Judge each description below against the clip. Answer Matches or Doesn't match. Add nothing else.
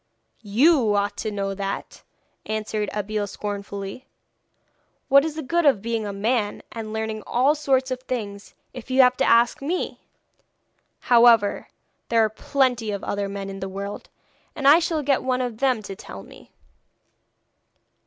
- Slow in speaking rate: Doesn't match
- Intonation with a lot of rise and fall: Doesn't match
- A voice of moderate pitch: Doesn't match